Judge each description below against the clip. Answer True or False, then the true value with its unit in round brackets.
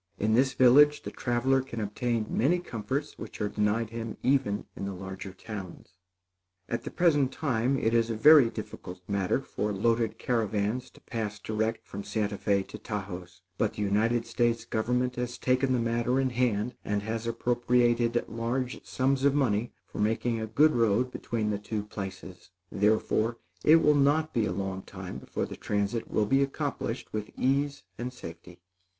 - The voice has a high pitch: False (115 Hz)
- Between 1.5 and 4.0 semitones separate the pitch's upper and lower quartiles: True (3.5 semitones)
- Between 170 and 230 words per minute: True (175 wpm)